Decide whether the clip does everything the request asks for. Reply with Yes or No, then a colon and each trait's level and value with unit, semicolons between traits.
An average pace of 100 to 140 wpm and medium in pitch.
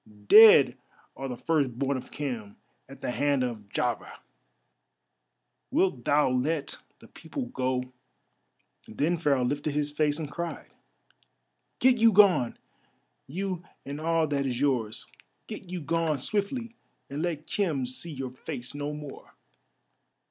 Yes: slow, 135 wpm; medium, 145 Hz